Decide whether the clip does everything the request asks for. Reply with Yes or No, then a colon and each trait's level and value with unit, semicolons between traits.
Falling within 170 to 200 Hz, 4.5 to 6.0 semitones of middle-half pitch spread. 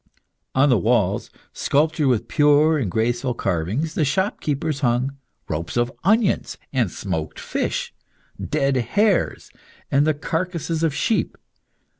No: medium, 140 Hz; average, 4.9 semitones